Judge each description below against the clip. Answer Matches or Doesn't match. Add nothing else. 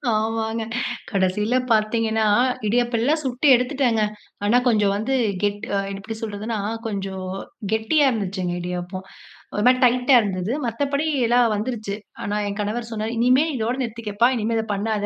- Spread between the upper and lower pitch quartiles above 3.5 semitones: Doesn't match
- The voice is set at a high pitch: Matches